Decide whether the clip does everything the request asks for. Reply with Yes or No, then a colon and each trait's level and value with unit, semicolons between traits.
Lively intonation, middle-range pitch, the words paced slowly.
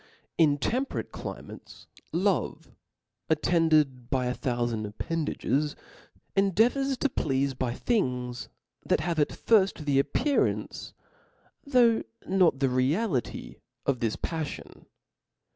Yes: wide, 7.2 semitones; medium, 150 Hz; slow, 110 wpm